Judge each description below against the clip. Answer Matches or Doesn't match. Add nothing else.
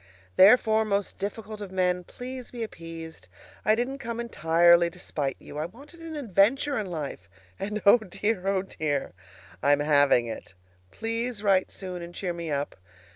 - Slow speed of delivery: Doesn't match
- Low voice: Doesn't match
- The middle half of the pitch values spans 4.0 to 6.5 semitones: Matches